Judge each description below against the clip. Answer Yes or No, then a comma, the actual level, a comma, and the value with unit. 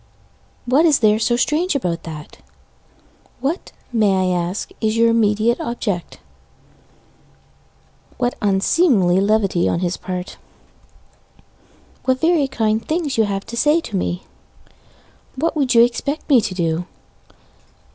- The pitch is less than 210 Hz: No, high, 225 Hz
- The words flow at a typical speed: No, slow, 120 wpm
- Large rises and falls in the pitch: Yes, wide, 5.9 semitones